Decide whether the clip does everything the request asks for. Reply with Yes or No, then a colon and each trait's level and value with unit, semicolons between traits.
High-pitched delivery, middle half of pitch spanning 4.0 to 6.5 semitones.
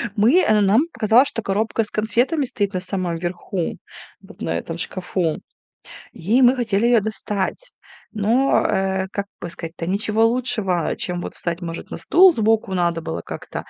Yes: high, 205 Hz; average, 4.4 semitones